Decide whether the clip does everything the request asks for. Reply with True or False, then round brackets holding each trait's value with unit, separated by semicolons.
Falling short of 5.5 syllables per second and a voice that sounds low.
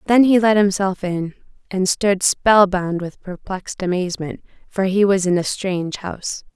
False (4.8 syllables/s; 190 Hz)